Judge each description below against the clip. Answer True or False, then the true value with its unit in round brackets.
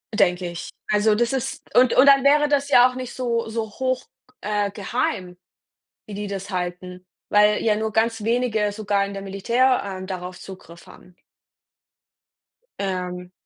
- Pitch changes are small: False (4.1 semitones)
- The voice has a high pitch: True (210 Hz)